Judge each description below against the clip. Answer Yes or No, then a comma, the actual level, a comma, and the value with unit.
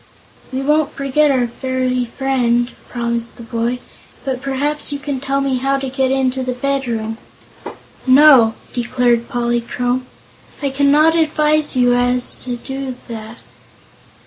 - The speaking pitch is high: Yes, very high, 260 Hz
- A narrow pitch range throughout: Yes, narrow, 2.3 semitones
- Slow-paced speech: Yes, slow, 130 wpm